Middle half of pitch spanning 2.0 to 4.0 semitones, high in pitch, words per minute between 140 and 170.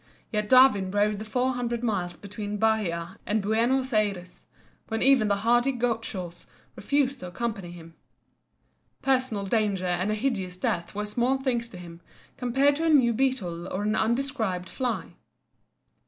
No: average, 4.7 semitones; high, 220 Hz; average, 155 wpm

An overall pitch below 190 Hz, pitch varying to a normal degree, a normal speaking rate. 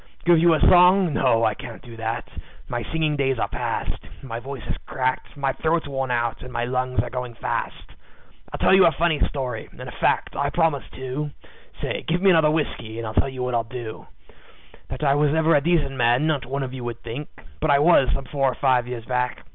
No: low, 135 Hz; average, 3.9 semitones; fast, 225 wpm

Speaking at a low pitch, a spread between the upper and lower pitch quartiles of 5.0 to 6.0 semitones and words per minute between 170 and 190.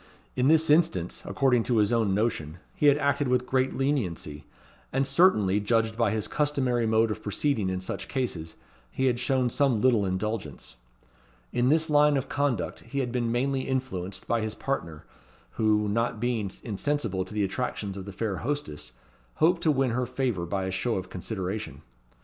Yes: low, 115 Hz; average, 5.3 semitones; average, 180 wpm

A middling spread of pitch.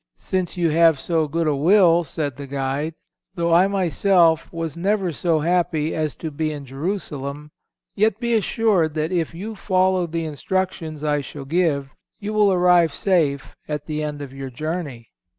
Yes: average, 3.5 semitones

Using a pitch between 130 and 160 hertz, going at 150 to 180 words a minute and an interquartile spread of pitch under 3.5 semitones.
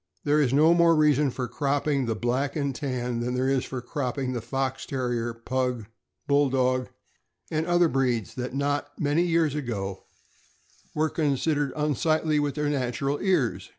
Yes: low, 135 Hz; average, 155 wpm; average, 3.1 semitones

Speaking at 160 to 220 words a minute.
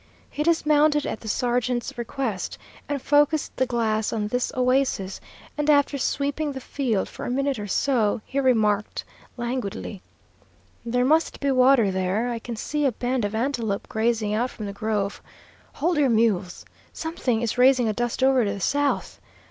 Yes: average, 165 wpm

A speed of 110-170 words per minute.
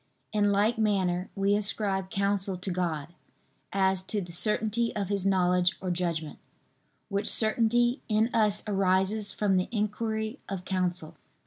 Yes: average, 140 wpm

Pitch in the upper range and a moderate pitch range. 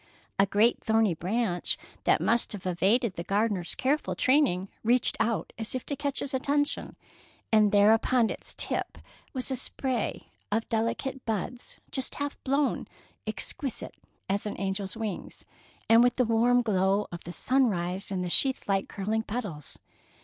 Yes: high, 225 Hz; average, 4.4 semitones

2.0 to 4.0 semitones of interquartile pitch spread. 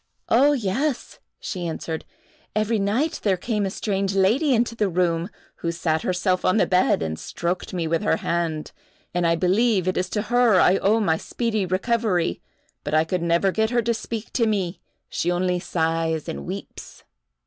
No: average, 4.4 semitones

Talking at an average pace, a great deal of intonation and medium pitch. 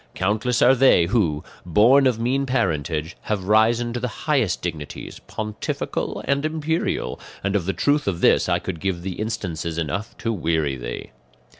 No: average, 165 wpm; wide, 6.3 semitones; low, 105 Hz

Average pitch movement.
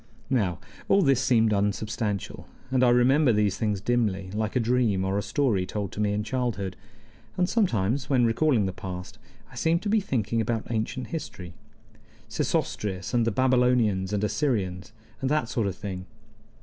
Yes: average, 4.2 semitones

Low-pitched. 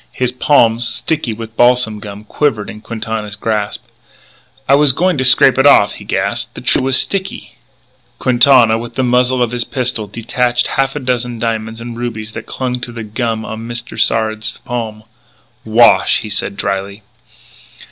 Yes: low, 120 Hz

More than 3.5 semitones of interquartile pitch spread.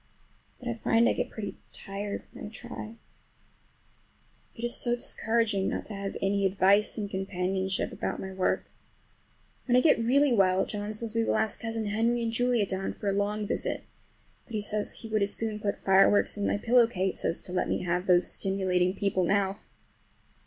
No: average, 2.8 semitones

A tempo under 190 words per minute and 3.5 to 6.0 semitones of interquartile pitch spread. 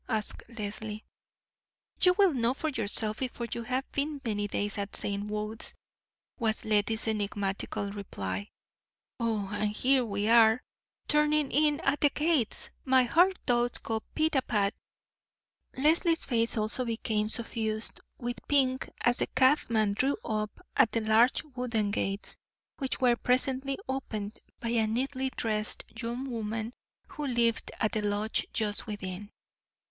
Yes: average, 140 wpm; average, 3.8 semitones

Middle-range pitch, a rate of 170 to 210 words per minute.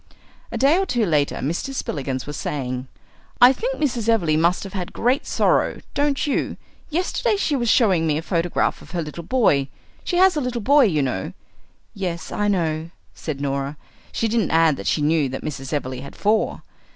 Yes: medium, 175 Hz; average, 195 wpm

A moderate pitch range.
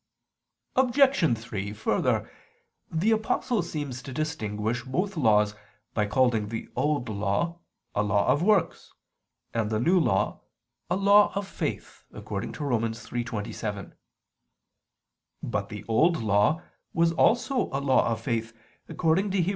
No: wide, 8.2 semitones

